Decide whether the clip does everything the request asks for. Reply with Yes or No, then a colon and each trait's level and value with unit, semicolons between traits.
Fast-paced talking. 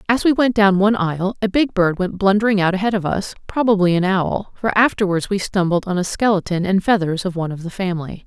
Yes: fast, 230 wpm